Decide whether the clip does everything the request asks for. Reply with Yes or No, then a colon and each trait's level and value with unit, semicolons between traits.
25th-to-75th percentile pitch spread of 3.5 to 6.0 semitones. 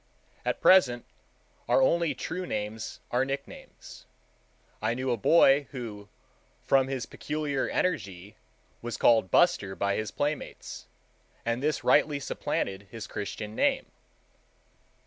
Yes: average, 5.2 semitones